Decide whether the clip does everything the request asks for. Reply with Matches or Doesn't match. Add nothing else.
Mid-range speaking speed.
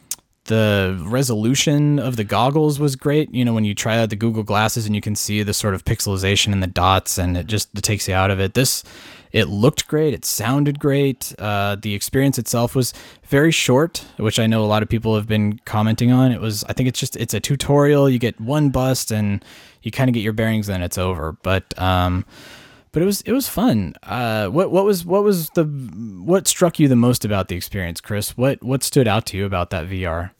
Doesn't match